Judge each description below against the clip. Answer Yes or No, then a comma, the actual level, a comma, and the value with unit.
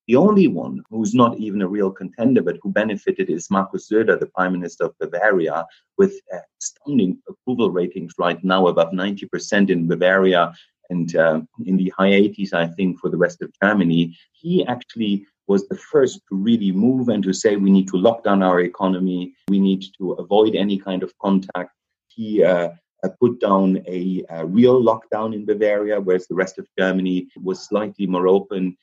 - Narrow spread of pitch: Yes, narrow, 2.2 semitones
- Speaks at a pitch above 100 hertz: No, very low, 95 Hz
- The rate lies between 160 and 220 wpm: Yes, average, 185 wpm